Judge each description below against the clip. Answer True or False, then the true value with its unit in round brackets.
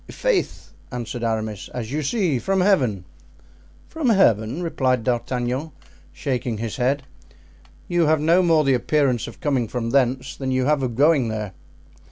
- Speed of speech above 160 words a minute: False (155 wpm)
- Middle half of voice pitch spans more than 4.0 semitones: True (4.6 semitones)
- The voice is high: False (130 Hz)